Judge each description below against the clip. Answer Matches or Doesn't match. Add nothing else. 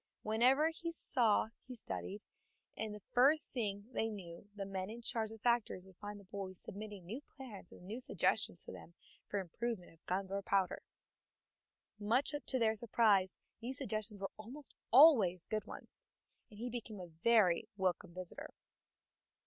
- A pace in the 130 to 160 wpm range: Doesn't match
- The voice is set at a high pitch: Matches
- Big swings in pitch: Doesn't match